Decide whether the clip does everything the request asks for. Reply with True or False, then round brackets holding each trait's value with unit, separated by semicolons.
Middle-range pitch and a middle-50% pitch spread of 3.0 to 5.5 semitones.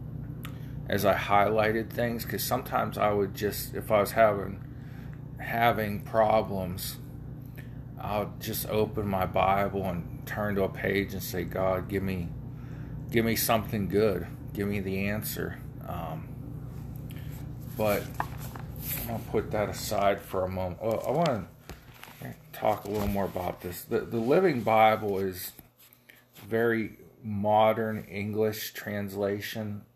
False (110 Hz; 4.5 semitones)